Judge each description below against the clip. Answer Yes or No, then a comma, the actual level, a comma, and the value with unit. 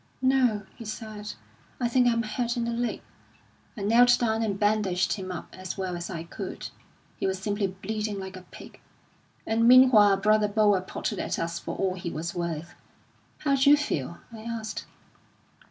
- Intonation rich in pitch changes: No, average, 3.7 semitones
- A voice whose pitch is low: No, high, 210 Hz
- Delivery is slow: No, average, 175 wpm